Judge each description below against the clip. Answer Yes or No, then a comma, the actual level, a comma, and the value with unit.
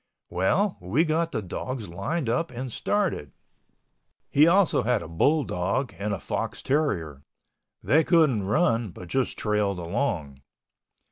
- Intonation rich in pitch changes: Yes, wide, 9.0 semitones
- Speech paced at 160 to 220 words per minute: No, average, 140 wpm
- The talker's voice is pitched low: Yes, low, 120 Hz